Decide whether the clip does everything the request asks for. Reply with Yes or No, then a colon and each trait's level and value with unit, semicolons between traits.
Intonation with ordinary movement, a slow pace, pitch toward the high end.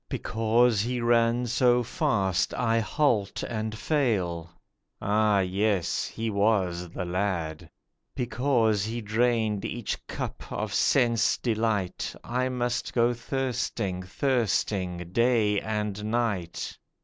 No: average, 3.6 semitones; slow, 110 wpm; low, 110 Hz